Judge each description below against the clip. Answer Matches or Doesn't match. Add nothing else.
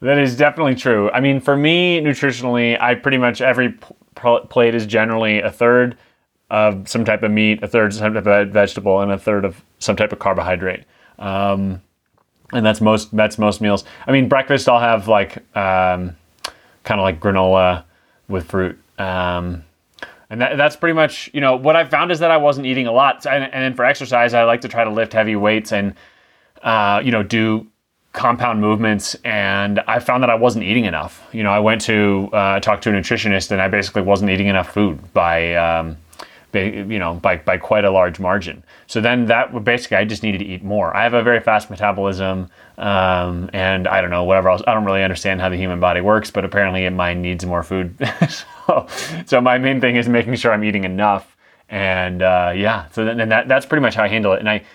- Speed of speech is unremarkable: Doesn't match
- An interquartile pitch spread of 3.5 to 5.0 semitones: Matches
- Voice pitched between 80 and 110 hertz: Matches